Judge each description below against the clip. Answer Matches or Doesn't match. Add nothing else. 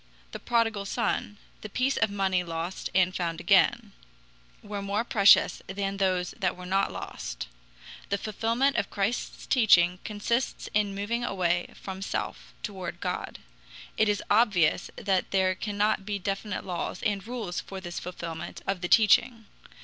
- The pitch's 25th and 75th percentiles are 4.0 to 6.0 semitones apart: Doesn't match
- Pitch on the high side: Matches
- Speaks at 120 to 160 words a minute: Matches